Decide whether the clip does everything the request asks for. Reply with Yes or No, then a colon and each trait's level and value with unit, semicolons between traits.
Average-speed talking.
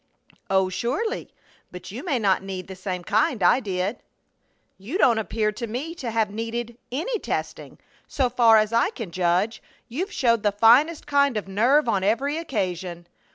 Yes: average, 170 wpm